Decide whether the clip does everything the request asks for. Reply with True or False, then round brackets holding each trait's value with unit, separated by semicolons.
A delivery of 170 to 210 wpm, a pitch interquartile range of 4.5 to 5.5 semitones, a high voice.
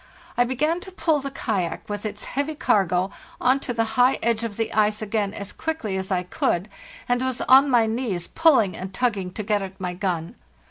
True (205 wpm; 5.0 semitones; 220 Hz)